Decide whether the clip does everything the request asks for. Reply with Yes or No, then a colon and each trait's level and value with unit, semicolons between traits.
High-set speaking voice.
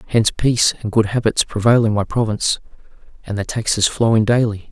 No: low, 110 Hz